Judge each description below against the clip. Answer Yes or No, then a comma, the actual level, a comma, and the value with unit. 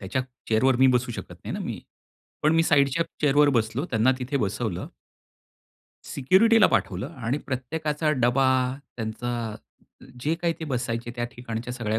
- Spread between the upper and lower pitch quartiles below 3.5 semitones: No, average, 4.2 semitones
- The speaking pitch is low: Yes, low, 125 Hz